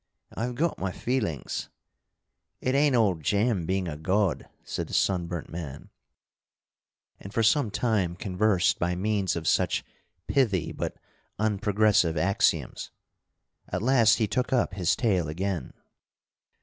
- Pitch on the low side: Yes, low, 100 Hz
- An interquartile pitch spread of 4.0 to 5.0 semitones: Yes, average, 4.3 semitones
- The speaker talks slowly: Yes, slow, 130 wpm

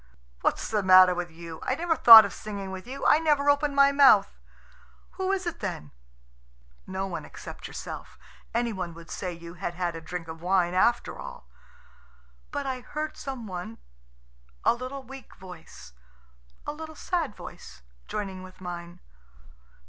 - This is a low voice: No, high, 200 Hz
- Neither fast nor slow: Yes, average, 165 wpm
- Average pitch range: No, wide, 7.7 semitones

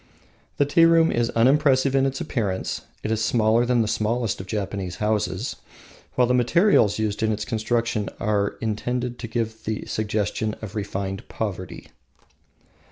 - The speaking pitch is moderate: No, low, 110 Hz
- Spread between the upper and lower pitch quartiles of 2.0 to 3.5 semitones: Yes, average, 2.8 semitones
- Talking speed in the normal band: Yes, average, 150 wpm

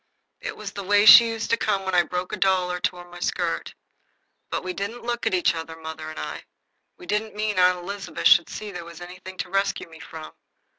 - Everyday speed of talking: No, fast, 230 wpm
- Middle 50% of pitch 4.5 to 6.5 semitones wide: No, average, 2.8 semitones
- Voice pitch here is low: No, medium, 185 Hz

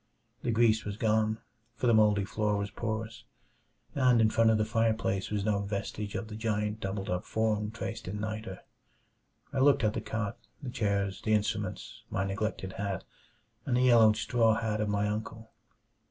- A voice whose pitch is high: No, low, 110 Hz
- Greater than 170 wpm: Yes, average, 180 wpm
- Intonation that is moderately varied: No, narrow, 1.5 semitones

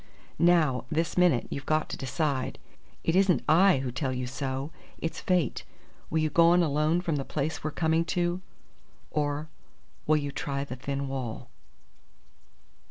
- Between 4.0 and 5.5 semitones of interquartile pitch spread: No, average, 3.4 semitones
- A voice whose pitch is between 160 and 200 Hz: No, medium, 150 Hz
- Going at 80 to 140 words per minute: No, average, 160 wpm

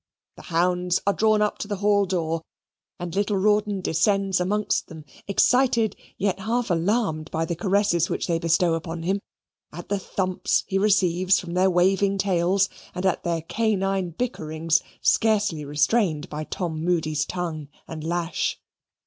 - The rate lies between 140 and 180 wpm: Yes, average, 155 wpm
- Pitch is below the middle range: No, medium, 180 Hz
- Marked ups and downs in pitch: No, average, 3.4 semitones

